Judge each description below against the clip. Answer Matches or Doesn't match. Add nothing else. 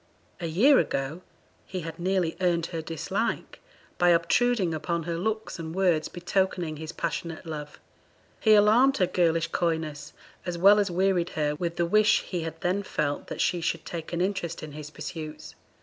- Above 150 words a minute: Matches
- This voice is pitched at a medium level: Matches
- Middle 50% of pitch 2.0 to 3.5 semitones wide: Matches